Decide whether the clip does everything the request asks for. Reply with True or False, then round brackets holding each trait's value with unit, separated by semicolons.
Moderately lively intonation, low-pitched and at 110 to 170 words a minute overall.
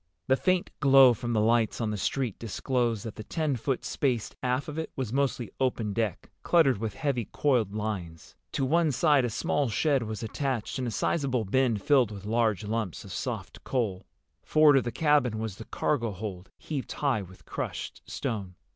False (4.1 semitones; 120 Hz; 190 wpm)